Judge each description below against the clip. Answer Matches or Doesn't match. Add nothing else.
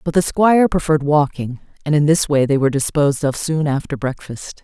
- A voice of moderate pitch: Matches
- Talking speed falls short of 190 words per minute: Doesn't match